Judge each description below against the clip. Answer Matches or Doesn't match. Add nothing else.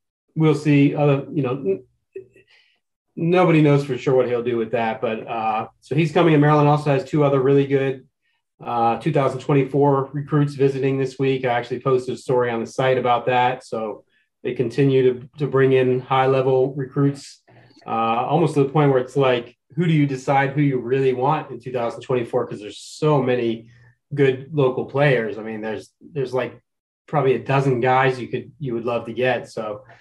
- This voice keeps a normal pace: Matches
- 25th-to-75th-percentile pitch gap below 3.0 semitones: Matches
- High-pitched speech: Doesn't match